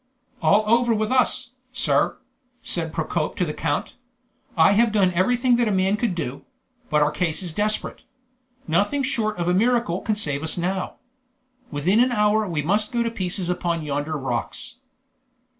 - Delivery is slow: No, average, 165 wpm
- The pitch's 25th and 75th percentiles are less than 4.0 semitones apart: No, wide, 5.4 semitones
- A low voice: No, high, 190 Hz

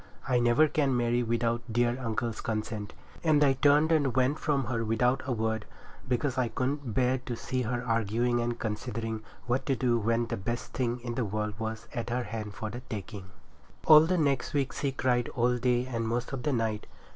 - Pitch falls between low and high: No, low, 120 Hz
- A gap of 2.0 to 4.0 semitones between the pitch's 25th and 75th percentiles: Yes, narrow, 2.5 semitones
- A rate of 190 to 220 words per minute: Yes, fast, 205 wpm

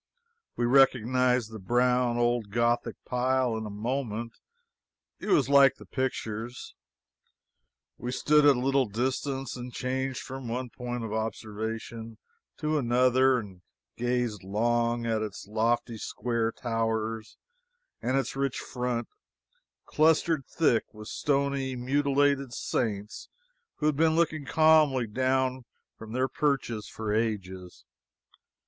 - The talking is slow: Yes, slow, 125 wpm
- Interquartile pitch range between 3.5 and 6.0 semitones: No, average, 3.0 semitones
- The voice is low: Yes, low, 125 Hz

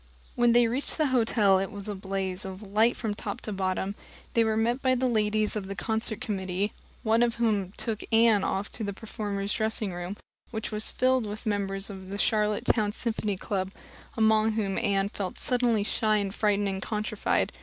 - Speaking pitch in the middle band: No, high, 210 Hz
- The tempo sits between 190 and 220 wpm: Yes, average, 195 wpm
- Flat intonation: Yes, narrow, 2.2 semitones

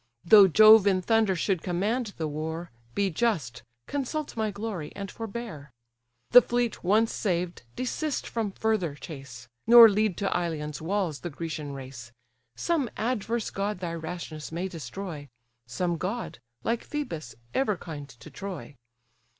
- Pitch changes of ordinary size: No, wide, 5.9 semitones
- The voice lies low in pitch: No, medium, 185 Hz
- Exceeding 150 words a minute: No, average, 140 wpm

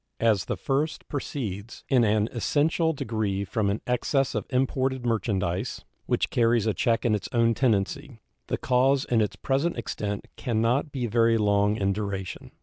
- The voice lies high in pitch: No, low, 115 Hz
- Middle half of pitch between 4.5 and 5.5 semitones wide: No, average, 4.1 semitones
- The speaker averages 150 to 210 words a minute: Yes, average, 165 wpm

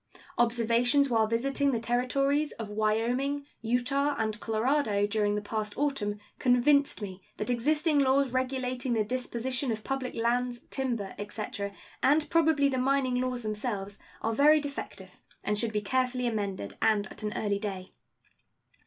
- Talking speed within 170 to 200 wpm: No, average, 145 wpm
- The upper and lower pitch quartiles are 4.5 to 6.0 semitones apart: No, average, 4.1 semitones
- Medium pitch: No, high, 240 Hz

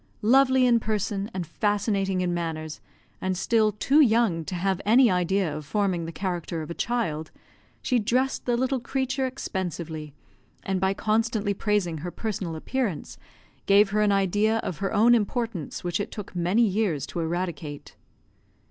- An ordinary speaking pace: Yes, average, 160 wpm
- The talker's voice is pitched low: No, high, 200 Hz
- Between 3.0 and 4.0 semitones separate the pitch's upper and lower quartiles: No, average, 4.5 semitones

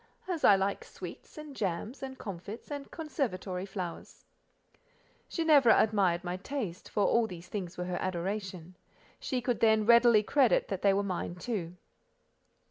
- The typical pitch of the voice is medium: No, high, 205 Hz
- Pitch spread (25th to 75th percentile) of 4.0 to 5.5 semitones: Yes, average, 5.2 semitones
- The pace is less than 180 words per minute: Yes, average, 150 wpm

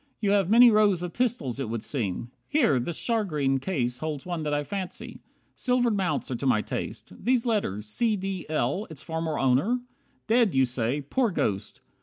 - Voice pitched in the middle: Yes, medium, 160 Hz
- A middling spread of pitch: No, wide, 8.1 semitones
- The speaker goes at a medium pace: Yes, average, 185 wpm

